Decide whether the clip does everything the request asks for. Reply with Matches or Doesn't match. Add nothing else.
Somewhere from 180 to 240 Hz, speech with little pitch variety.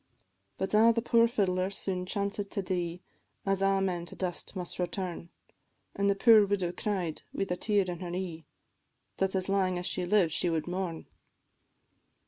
Matches